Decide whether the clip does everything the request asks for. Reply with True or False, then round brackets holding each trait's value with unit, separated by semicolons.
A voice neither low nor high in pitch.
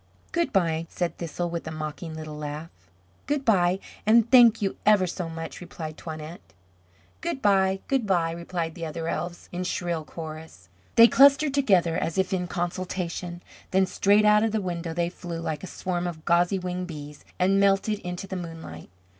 True (175 Hz)